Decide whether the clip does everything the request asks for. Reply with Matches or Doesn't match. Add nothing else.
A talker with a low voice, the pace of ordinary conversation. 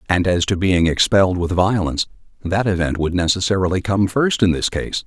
Matches